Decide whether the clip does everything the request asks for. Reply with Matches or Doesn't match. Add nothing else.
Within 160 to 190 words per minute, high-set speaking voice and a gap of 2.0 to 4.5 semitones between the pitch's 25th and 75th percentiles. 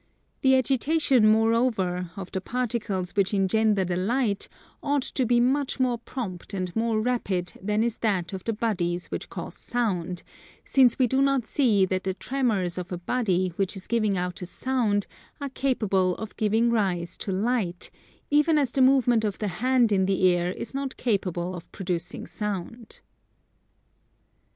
Doesn't match